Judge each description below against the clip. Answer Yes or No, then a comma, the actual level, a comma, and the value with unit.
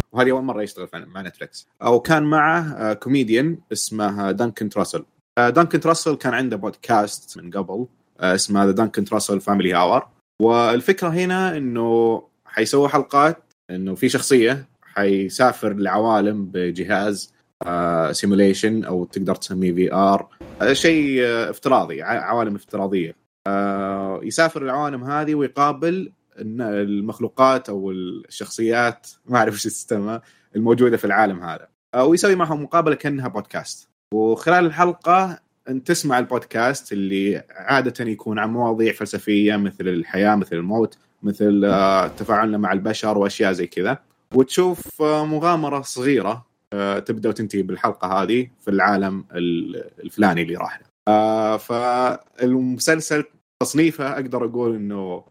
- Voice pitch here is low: Yes, low, 115 Hz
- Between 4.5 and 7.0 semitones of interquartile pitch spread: Yes, average, 5.2 semitones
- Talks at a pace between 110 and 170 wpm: Yes, average, 115 wpm